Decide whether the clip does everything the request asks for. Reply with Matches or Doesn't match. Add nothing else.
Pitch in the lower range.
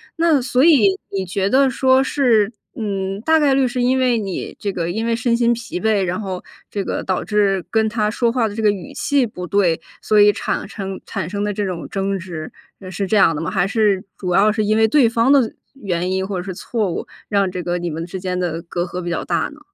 Doesn't match